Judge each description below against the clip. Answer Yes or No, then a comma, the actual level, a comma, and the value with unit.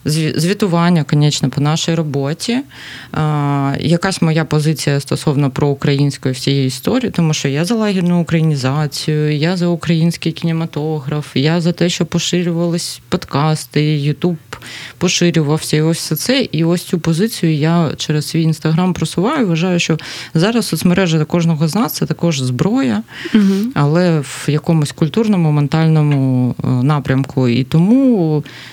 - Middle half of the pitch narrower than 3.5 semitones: Yes, average, 2.9 semitones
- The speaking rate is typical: Yes, average, 125 wpm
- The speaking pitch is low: No, medium, 160 Hz